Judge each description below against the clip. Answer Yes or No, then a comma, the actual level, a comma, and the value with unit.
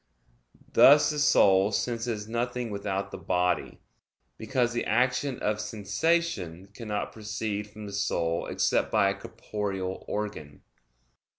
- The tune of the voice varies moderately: Yes, average, 3.6 semitones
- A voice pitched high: No, low, 105 Hz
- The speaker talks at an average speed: No, slow, 120 wpm